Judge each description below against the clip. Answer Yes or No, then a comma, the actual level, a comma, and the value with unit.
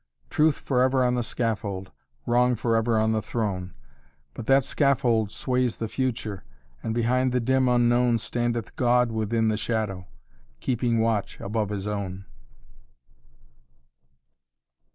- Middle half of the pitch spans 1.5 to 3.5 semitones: Yes, narrow, 2.4 semitones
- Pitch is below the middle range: Yes, low, 115 Hz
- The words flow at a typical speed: No, slow, 125 wpm